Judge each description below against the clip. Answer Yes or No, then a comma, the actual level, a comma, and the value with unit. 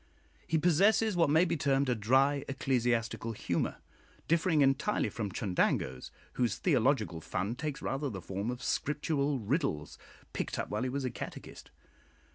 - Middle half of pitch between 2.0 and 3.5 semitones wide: No, average, 4.8 semitones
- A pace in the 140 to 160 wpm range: Yes, average, 150 wpm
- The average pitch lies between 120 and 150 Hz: Yes, low, 135 Hz